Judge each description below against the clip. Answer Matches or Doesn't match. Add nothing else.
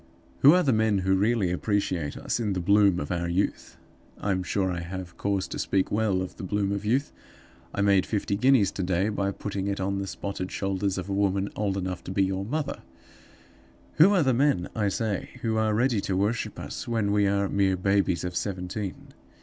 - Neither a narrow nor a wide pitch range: Doesn't match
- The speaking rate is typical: Doesn't match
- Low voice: Matches